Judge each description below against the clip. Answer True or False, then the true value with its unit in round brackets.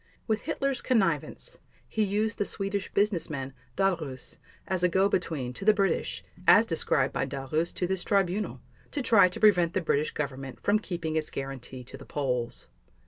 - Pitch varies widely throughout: True (6.3 semitones)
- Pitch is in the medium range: True (180 Hz)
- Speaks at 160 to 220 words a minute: True (170 wpm)